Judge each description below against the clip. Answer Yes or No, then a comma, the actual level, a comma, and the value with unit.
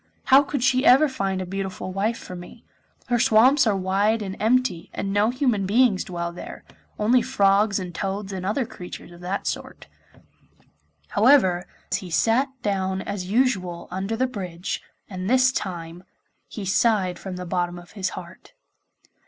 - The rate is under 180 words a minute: Yes, average, 160 wpm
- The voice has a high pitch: Yes, high, 195 Hz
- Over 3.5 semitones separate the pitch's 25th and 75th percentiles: Yes, average, 4.2 semitones